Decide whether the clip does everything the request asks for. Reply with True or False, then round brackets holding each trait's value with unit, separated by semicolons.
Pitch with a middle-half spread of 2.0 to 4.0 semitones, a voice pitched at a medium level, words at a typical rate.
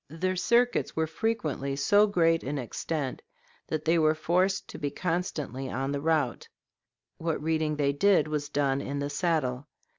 True (3.4 semitones; 155 Hz; 160 wpm)